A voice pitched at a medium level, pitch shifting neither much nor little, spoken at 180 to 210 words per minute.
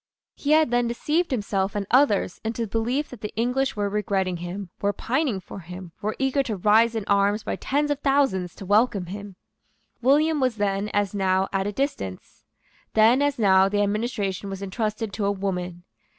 No: high, 210 Hz; average, 4.3 semitones; average, 190 wpm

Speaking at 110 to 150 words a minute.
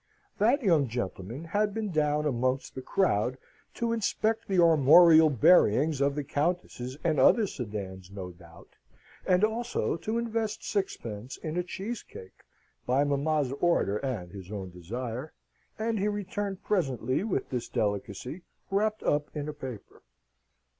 Yes: average, 145 wpm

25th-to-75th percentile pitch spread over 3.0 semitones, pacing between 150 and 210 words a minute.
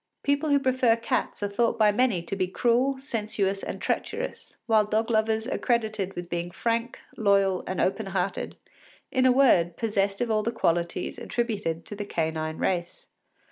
Yes: average, 4.0 semitones; average, 175 wpm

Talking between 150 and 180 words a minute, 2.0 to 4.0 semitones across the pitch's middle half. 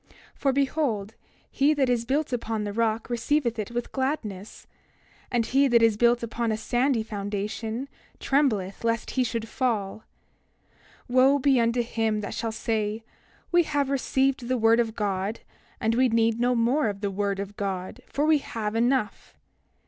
Yes: average, 170 wpm; average, 3.3 semitones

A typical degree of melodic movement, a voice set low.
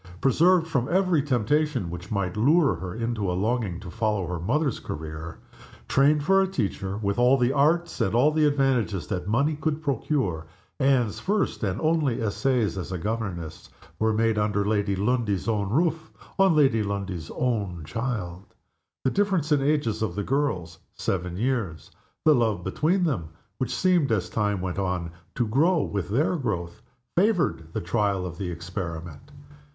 No: wide, 7.4 semitones; low, 110 Hz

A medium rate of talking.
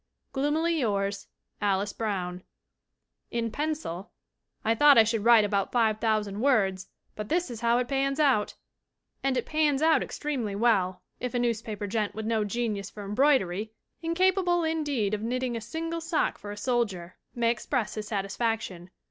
Yes: average, 160 wpm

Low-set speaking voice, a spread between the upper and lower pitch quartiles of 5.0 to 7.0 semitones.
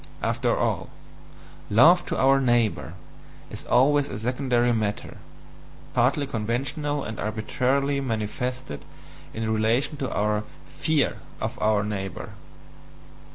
No: low, 120 Hz; average, 4.2 semitones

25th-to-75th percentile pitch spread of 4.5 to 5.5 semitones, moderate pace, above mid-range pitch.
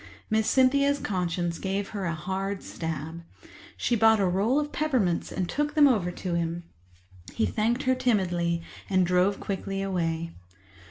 Yes: average, 4.9 semitones; average, 155 wpm; high, 195 Hz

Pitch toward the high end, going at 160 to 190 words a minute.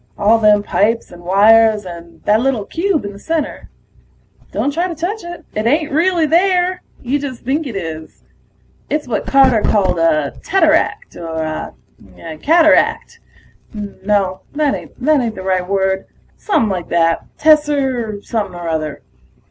No: high, 225 Hz; average, 150 wpm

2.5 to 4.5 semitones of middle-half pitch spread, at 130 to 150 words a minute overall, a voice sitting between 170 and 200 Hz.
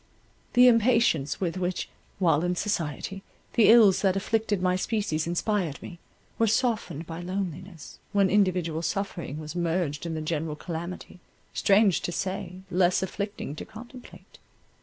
Yes: average, 3.5 semitones; average, 140 wpm; medium, 185 Hz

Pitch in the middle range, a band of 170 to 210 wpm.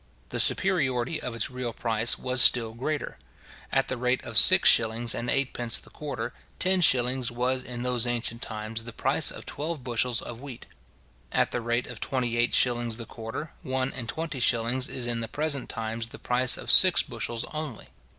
No: low, 125 Hz; average, 190 wpm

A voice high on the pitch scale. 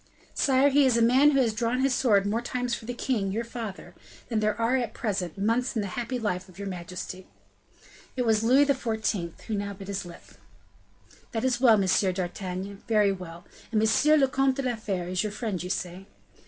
Yes: high, 220 Hz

